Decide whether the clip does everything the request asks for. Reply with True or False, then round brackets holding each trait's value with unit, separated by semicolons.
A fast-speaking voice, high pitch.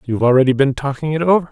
False (235 wpm; 140 Hz)